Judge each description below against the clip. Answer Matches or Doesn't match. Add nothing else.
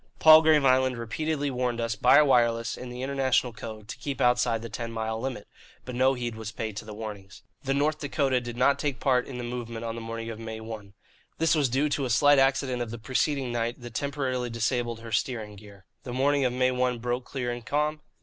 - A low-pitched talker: Matches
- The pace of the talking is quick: Matches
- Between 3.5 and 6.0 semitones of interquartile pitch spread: Doesn't match